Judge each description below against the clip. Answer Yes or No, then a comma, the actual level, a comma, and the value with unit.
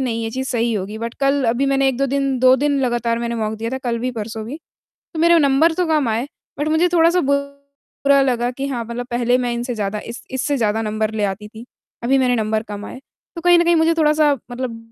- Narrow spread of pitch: No, average, 3.5 semitones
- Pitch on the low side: No, very high, 250 Hz